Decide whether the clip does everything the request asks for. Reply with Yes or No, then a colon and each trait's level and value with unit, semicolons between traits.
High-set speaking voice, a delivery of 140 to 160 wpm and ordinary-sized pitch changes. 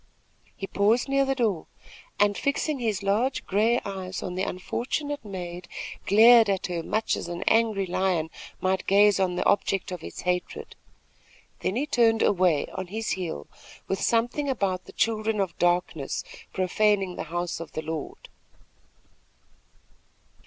Yes: high, 195 Hz; average, 150 wpm; average, 3.8 semitones